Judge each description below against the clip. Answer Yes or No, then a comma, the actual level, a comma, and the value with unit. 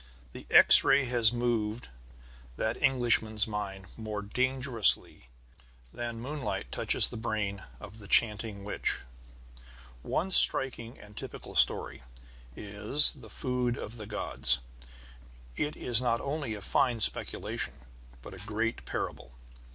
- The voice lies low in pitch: Yes, low, 115 Hz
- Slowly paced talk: Yes, slow, 125 wpm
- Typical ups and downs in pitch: Yes, average, 3.1 semitones